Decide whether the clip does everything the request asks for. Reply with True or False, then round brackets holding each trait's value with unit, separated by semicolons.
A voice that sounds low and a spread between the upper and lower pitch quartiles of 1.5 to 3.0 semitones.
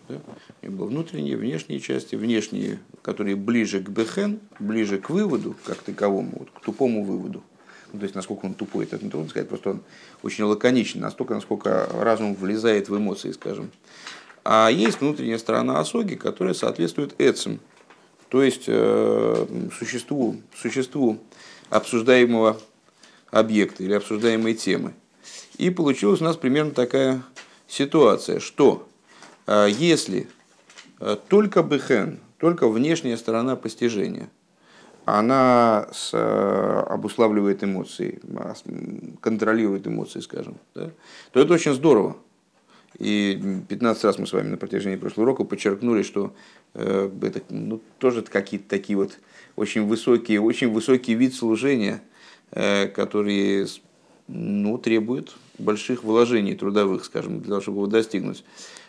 False (110 Hz; 3.7 semitones)